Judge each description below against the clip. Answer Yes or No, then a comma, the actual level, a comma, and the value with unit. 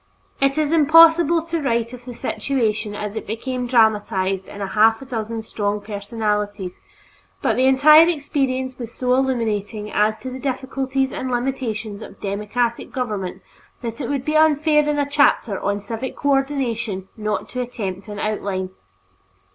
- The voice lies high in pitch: Yes, high, 240 Hz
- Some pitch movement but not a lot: Yes, average, 4.4 semitones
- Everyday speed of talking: Yes, average, 155 wpm